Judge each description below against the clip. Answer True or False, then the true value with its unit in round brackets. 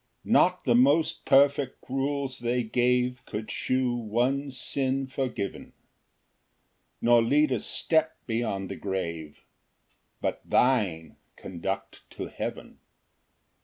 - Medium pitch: False (125 Hz)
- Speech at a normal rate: False (110 wpm)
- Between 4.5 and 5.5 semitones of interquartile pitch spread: False (3.7 semitones)